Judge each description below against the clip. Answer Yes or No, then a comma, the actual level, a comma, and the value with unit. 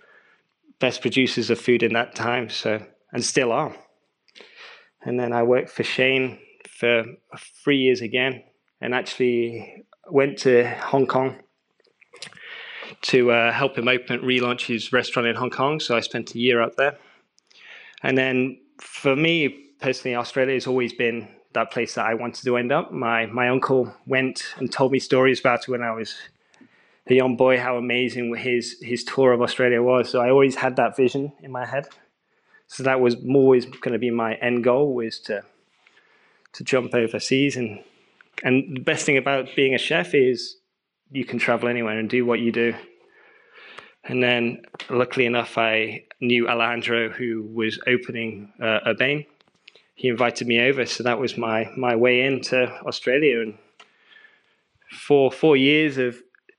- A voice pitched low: Yes, low, 125 Hz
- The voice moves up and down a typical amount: No, narrow, 1.9 semitones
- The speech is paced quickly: No, average, 170 wpm